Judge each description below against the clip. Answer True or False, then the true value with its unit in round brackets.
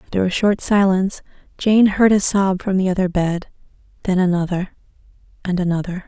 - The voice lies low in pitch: False (190 Hz)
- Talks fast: False (160 wpm)